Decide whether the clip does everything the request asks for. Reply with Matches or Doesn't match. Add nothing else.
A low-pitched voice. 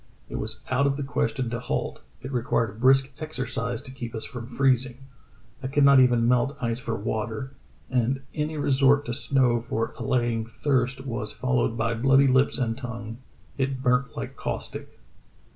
Matches